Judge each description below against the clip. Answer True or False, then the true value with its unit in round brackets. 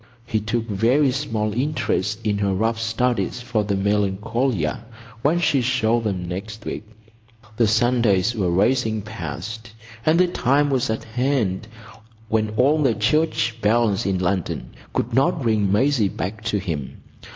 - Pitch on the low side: True (110 Hz)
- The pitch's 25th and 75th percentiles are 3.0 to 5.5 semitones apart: True (3.6 semitones)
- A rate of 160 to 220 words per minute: False (150 wpm)